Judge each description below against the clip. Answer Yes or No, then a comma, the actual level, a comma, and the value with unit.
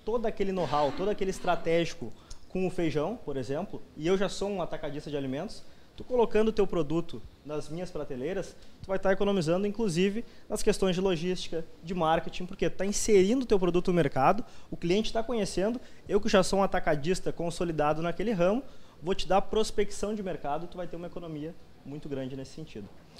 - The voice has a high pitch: No, medium, 180 Hz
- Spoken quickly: Yes, fast, 195 wpm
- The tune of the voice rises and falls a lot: No, average, 4.2 semitones